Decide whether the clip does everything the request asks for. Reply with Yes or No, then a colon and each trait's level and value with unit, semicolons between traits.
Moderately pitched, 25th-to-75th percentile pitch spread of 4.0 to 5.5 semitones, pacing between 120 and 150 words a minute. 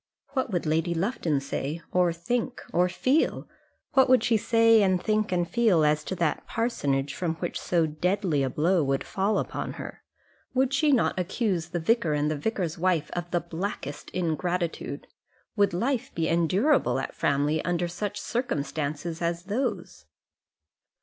No: medium, 175 Hz; average, 5.2 semitones; average, 160 wpm